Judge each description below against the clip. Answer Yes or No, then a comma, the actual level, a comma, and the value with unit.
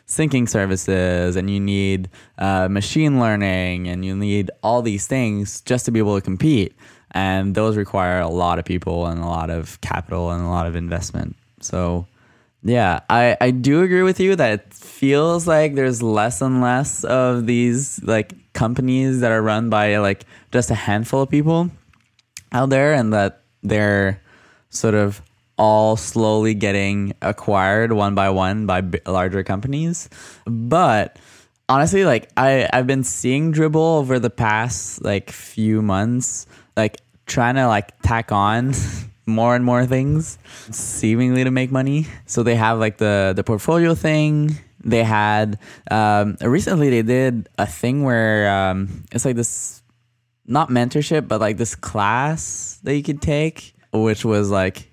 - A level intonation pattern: No, average, 4.2 semitones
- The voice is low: Yes, low, 110 Hz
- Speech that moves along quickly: No, average, 160 wpm